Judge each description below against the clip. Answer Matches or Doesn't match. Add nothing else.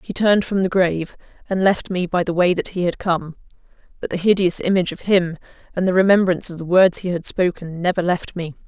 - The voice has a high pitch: Doesn't match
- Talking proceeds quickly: Matches